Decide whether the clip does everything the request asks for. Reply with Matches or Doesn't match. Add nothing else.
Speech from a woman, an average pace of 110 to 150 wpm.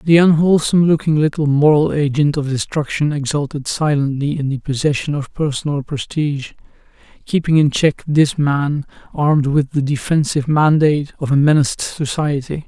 Doesn't match